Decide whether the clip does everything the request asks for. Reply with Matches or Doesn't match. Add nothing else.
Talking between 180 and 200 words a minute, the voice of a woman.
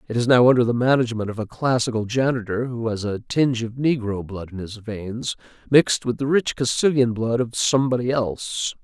Doesn't match